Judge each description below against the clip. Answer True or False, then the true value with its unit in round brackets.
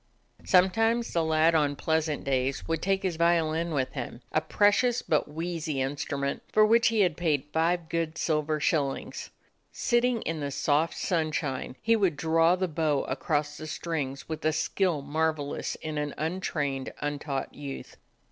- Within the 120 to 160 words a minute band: True (155 wpm)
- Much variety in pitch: False (3.0 semitones)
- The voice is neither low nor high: True (160 Hz)